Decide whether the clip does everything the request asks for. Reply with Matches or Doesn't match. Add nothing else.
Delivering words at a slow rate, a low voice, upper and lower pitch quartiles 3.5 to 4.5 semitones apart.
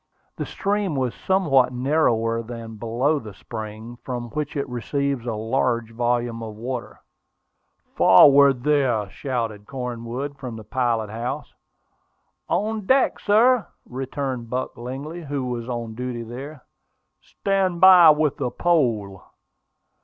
Matches